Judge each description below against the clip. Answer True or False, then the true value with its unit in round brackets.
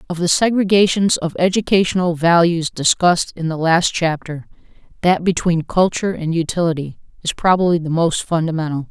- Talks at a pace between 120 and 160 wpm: True (140 wpm)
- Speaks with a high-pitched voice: False (170 Hz)